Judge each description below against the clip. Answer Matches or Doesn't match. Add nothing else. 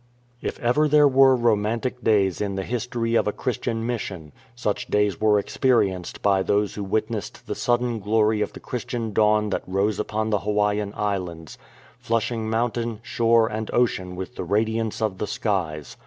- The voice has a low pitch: Matches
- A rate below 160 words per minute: Doesn't match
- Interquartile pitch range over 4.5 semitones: Doesn't match